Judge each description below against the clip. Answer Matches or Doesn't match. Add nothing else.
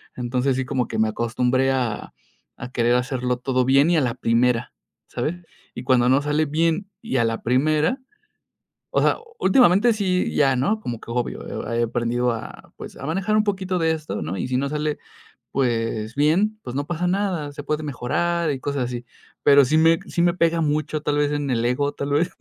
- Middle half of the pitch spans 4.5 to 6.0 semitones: Matches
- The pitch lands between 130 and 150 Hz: Matches